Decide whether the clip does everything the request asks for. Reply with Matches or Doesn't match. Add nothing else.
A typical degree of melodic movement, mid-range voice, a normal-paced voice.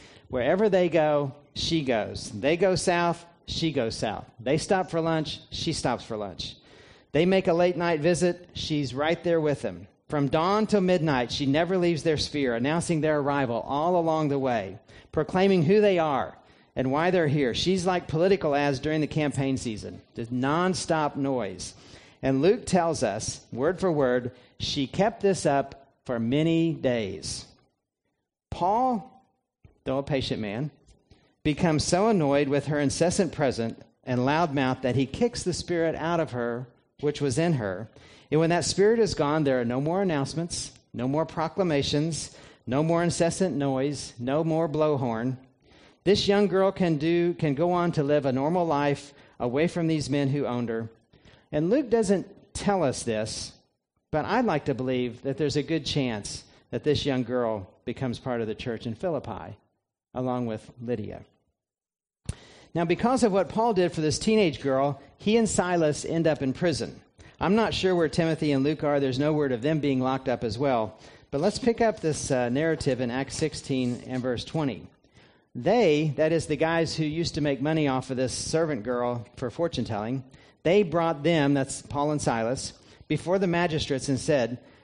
Matches